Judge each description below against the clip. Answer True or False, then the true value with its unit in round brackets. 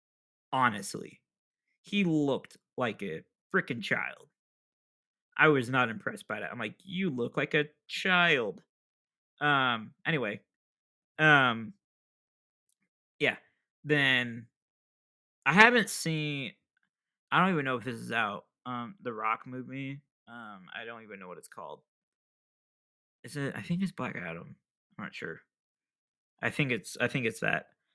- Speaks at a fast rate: False (140 wpm)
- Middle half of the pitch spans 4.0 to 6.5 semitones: True (4.4 semitones)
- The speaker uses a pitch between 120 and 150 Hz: True (140 Hz)